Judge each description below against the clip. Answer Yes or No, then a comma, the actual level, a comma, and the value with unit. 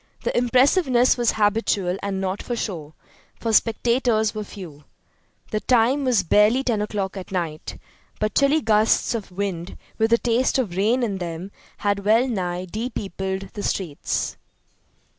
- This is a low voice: No, high, 210 Hz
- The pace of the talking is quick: No, average, 150 wpm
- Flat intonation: No, average, 3.8 semitones